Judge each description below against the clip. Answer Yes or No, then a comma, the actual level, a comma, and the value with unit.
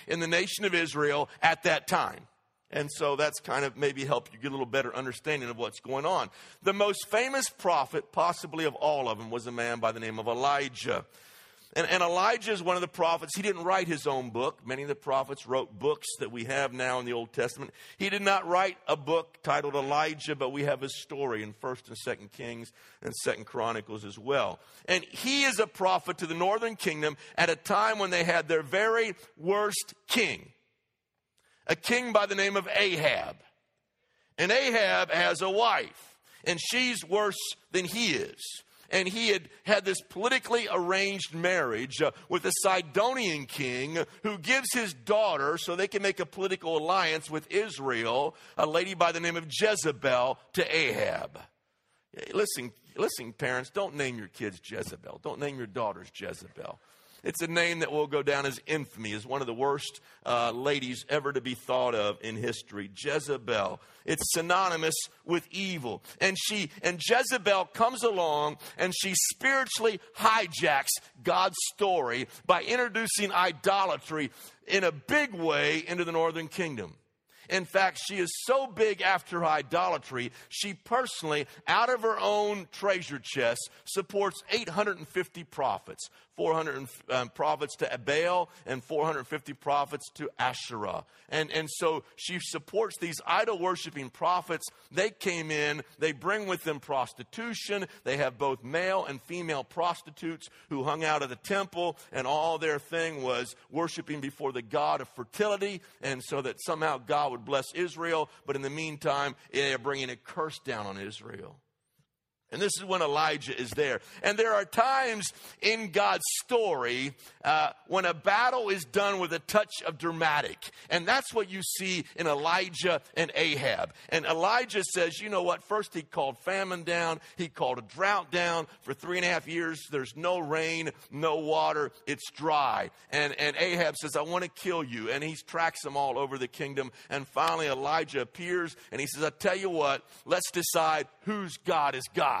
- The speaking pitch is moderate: Yes, medium, 165 Hz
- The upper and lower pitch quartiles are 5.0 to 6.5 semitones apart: Yes, wide, 5.5 semitones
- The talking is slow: No, average, 175 wpm